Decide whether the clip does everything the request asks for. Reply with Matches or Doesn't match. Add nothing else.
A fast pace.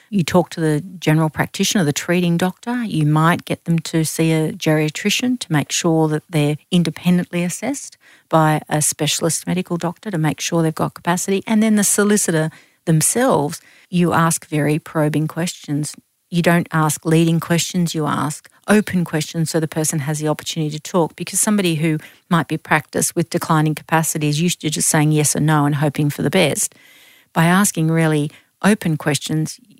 Doesn't match